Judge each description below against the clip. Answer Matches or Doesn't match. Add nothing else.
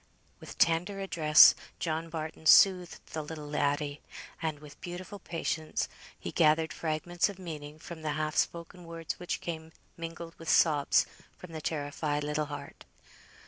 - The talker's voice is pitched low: Doesn't match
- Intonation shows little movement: Matches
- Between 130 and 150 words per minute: Matches